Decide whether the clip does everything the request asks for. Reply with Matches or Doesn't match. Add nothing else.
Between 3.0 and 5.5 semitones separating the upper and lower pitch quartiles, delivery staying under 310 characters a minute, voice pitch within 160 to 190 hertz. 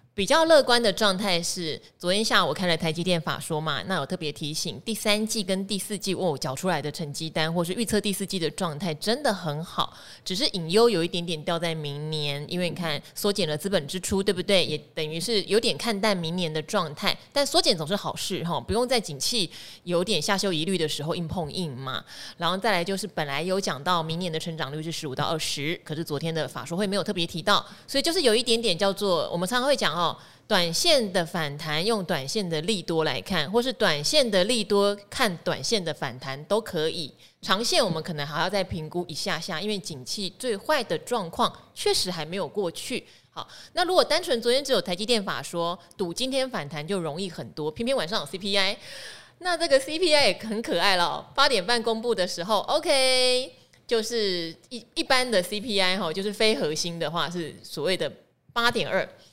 Doesn't match